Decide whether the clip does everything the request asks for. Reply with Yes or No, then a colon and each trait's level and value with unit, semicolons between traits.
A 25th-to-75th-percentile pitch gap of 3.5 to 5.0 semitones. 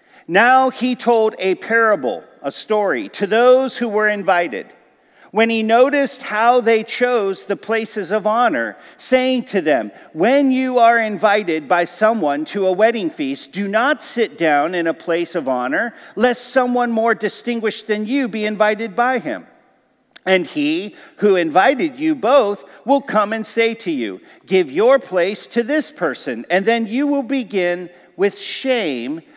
Yes: average, 4.2 semitones